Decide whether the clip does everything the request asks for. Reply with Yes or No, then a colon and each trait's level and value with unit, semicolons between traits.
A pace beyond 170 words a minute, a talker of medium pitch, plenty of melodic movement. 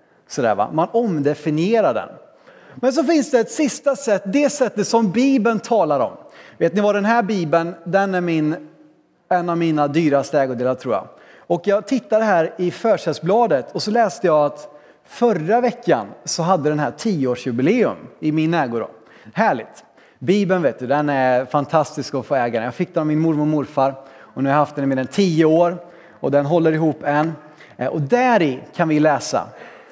Yes: average, 185 wpm; medium, 165 Hz; wide, 6.2 semitones